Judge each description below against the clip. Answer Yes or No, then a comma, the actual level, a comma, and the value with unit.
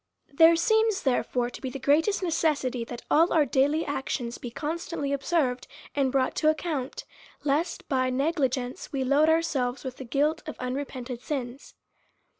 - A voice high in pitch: Yes, very high, 280 Hz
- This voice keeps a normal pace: Yes, average, 160 wpm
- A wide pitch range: No, average, 3.9 semitones